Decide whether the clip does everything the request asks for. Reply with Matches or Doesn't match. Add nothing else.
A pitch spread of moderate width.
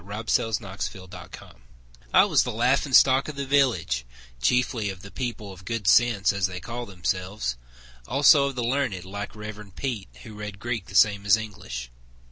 Matches